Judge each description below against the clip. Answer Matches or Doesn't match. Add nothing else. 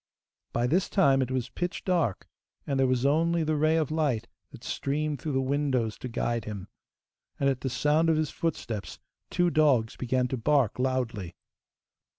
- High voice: Doesn't match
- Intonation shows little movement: Doesn't match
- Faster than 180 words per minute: Doesn't match